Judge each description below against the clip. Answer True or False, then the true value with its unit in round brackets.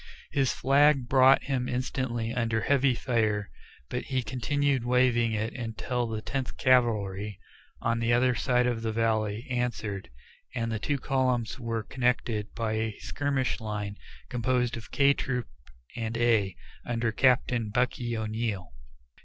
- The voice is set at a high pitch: False (120 Hz)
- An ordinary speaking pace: True (145 wpm)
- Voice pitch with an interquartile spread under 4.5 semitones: True (2.4 semitones)